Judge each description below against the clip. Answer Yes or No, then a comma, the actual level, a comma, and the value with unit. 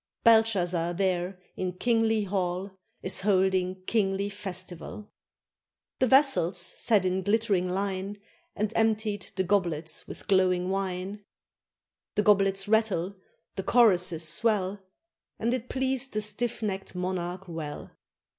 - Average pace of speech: No, slow, 115 wpm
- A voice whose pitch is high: Yes, high, 195 Hz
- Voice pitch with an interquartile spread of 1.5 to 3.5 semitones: Yes, average, 2.8 semitones